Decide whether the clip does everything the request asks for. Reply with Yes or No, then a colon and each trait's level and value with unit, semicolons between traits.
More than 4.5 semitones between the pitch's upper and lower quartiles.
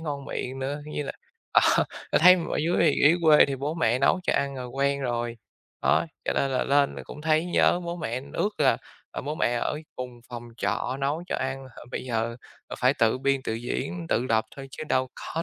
No: average, 3.4 semitones